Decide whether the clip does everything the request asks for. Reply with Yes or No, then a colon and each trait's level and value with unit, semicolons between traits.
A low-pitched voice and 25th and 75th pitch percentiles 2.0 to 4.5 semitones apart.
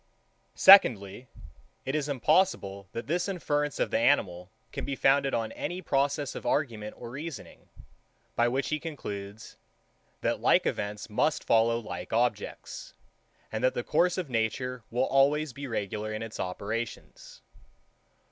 No: low, 125 Hz; average, 5.2 semitones